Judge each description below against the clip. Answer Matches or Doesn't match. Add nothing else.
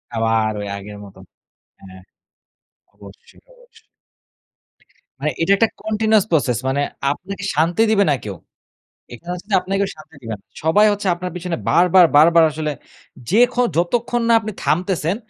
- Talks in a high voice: Doesn't match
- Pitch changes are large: Matches